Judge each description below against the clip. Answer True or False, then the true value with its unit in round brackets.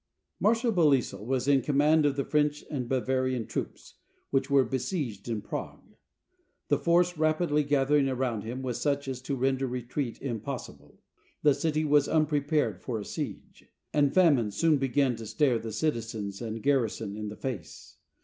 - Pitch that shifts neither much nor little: True (4.0 semitones)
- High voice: False (135 Hz)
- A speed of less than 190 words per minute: True (165 wpm)